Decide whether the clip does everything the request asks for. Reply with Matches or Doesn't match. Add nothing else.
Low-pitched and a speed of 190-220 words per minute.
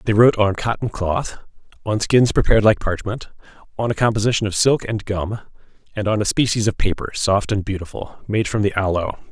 Matches